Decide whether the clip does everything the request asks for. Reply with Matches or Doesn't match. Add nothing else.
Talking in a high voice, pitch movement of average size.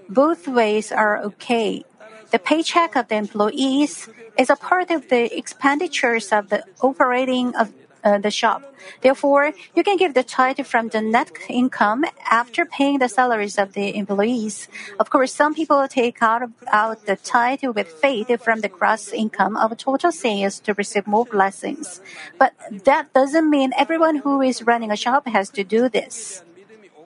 Matches